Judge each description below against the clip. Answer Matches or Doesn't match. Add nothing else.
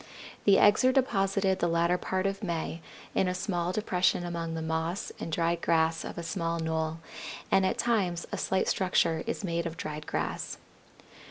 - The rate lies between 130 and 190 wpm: Matches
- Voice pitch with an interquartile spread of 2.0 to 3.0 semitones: Matches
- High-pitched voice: Doesn't match